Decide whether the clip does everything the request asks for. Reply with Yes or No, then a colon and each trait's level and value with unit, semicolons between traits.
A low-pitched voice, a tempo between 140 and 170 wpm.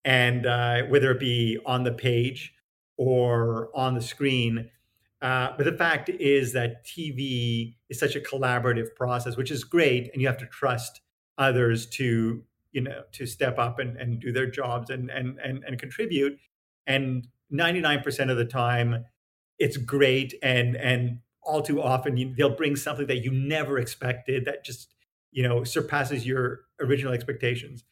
Yes: low, 130 Hz; average, 165 wpm